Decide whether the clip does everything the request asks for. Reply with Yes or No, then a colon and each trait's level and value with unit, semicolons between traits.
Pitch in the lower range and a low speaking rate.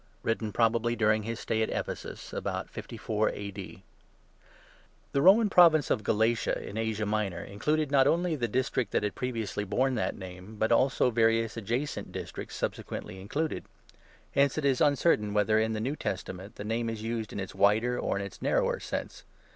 No: low, 115 Hz; average, 175 wpm